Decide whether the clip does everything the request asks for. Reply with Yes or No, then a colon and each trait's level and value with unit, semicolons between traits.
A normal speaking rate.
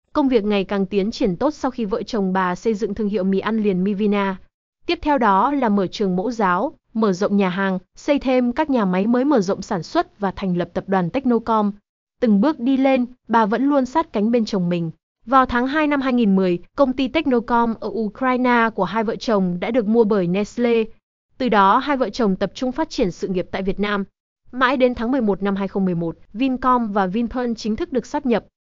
Yes: average, 225 wpm